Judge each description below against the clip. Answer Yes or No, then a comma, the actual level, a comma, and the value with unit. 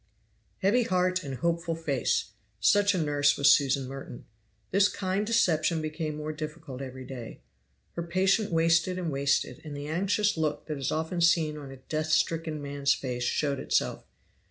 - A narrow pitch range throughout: No, average, 3.8 semitones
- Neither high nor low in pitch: Yes, medium, 155 Hz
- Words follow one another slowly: No, average, 165 wpm